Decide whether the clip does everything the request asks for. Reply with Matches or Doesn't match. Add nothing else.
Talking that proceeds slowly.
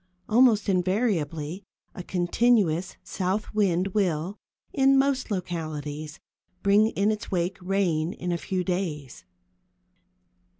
Matches